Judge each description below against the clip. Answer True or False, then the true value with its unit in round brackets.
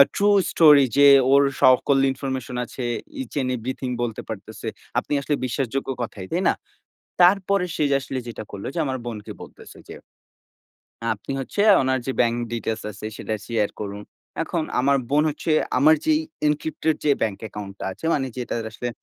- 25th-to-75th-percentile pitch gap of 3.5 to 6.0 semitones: True (4.5 semitones)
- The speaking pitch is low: True (130 Hz)